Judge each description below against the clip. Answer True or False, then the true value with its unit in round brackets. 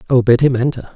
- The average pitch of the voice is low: True (125 Hz)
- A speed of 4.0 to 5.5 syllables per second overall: False (6.7 syllables/s)